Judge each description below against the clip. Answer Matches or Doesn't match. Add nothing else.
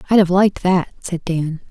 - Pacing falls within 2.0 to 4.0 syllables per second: Doesn't match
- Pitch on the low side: Doesn't match